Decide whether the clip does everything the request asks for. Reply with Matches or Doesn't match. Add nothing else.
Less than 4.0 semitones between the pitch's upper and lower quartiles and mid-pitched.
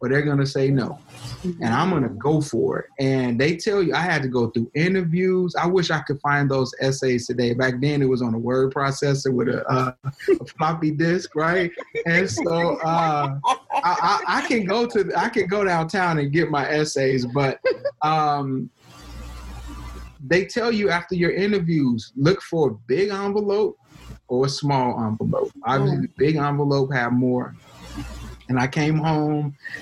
Doesn't match